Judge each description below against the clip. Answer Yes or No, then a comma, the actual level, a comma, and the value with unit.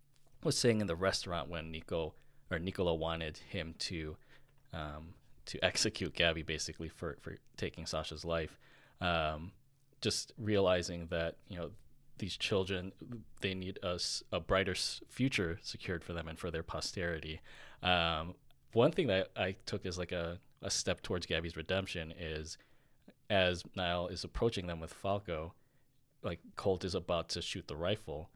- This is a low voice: Yes, very low, 90 Hz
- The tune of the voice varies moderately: Yes, average, 3.4 semitones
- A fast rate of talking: No, average, 155 wpm